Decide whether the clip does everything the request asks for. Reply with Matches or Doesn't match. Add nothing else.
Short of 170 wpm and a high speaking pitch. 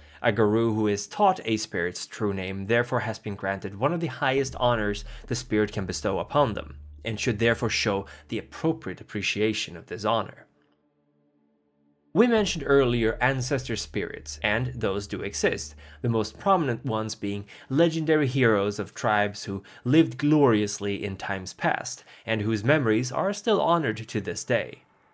Doesn't match